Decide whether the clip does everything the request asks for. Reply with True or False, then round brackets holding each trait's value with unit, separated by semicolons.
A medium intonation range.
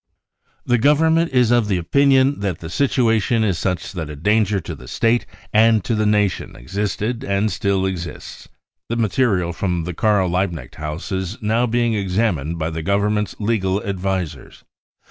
True (4.1 semitones)